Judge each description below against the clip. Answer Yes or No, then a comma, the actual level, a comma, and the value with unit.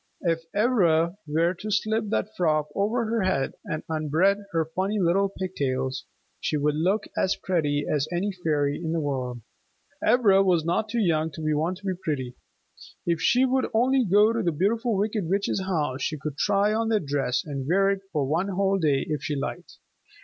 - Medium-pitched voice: Yes, medium, 175 Hz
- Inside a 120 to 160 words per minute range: No, average, 190 wpm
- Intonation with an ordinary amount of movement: Yes, average, 5.0 semitones